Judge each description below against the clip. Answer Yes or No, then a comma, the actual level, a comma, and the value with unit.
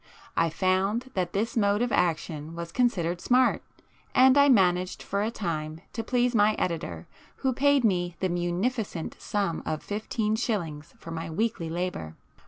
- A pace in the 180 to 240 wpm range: No, average, 160 wpm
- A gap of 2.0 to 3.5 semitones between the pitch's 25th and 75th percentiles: No, average, 5.3 semitones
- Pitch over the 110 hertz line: Yes, high, 190 Hz